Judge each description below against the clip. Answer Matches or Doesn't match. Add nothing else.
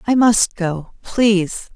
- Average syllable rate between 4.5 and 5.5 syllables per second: Doesn't match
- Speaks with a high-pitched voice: Matches